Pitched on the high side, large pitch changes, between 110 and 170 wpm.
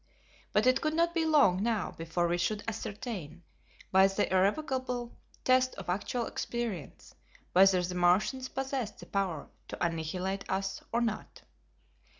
Yes: high, 200 Hz; wide, 5.7 semitones; average, 145 wpm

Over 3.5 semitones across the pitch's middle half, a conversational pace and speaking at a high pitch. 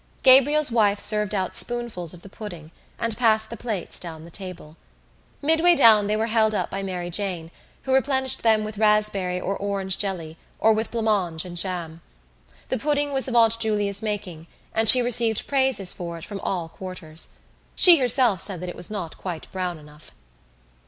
Yes: average, 4.4 semitones; average, 180 wpm; high, 205 Hz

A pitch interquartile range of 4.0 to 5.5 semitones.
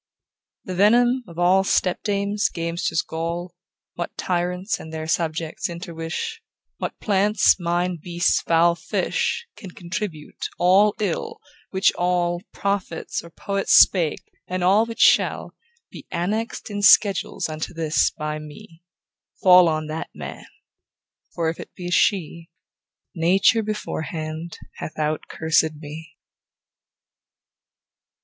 No: average, 3.4 semitones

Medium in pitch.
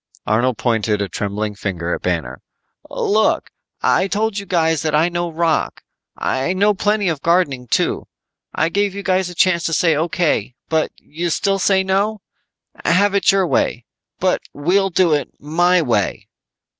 Yes: medium, 170 Hz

